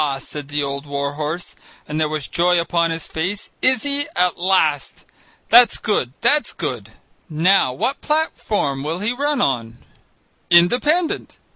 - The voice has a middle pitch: Yes, medium, 170 Hz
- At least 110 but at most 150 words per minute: Yes, average, 145 wpm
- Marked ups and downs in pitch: Yes, wide, 8.3 semitones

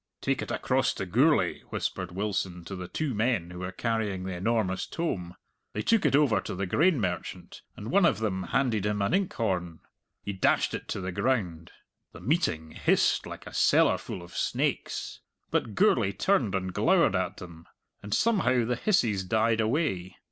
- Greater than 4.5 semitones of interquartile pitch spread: Yes, average, 5.2 semitones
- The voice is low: Yes, low, 100 Hz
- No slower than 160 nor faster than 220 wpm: Yes, average, 175 wpm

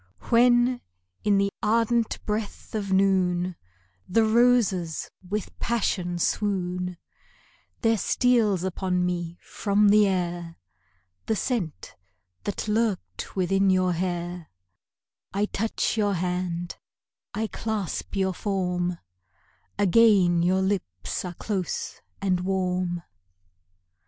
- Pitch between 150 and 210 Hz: Yes, high, 190 Hz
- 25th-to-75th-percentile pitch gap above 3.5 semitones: No, average, 2.9 semitones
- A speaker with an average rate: No, slow, 100 wpm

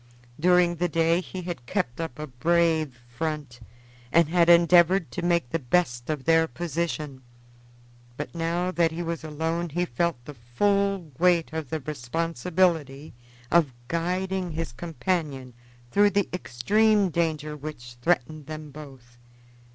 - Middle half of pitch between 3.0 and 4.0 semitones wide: Yes, average, 3.3 semitones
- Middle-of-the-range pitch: Yes, medium, 165 Hz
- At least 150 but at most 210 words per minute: No, average, 140 wpm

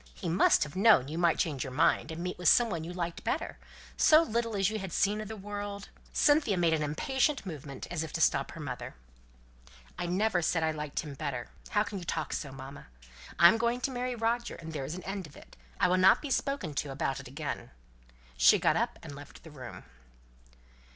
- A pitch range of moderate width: No, wide, 5.9 semitones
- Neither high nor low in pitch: Yes, medium, 175 Hz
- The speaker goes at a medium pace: No, fast, 220 wpm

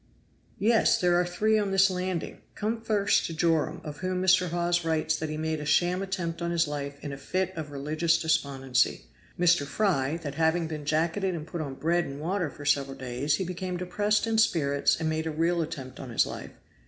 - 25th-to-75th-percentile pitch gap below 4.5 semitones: Yes, average, 3.4 semitones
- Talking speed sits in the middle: No, fast, 210 wpm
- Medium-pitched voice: Yes, medium, 165 Hz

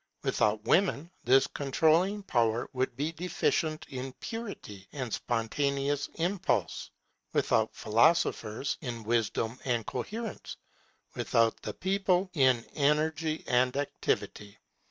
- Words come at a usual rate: No, slow, 105 wpm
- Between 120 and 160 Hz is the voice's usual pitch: Yes, medium, 140 Hz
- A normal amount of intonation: No, wide, 5.7 semitones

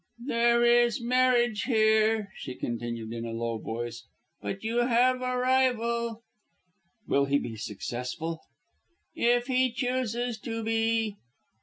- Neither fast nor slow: No, slow, 125 wpm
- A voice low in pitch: No, high, 230 Hz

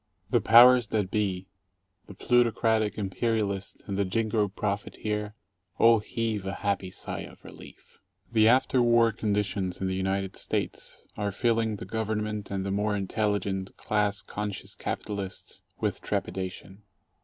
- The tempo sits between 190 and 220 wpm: No, average, 145 wpm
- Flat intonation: Yes, narrow, 2.3 semitones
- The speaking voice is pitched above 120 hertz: No, low, 105 Hz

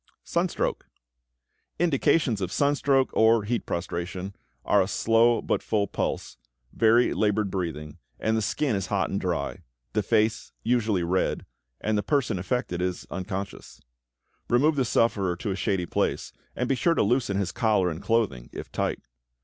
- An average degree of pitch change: Yes, average, 4.2 semitones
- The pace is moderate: Yes, average, 155 wpm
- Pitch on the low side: Yes, low, 105 Hz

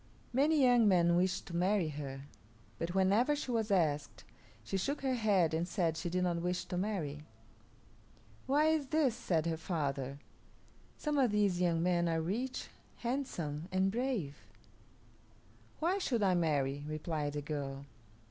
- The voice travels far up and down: Yes, wide, 6.8 semitones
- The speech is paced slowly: No, average, 155 wpm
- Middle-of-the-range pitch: Yes, medium, 180 Hz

